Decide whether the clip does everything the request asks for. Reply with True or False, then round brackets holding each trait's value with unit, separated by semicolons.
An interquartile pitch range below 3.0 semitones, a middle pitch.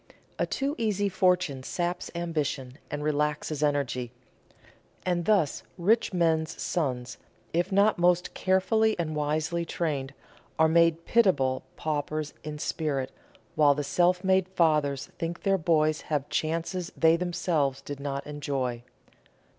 False (3.6 semitones; 160 Hz)